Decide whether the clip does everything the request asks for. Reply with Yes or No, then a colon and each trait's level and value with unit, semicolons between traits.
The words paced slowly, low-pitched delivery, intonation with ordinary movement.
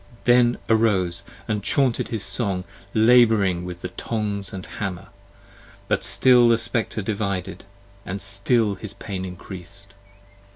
Yes: slow, 125 wpm; low, 100 Hz; average, 3.3 semitones